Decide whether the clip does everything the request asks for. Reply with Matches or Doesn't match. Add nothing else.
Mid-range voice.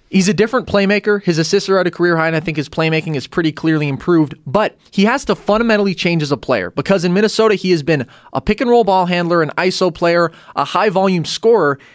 Matches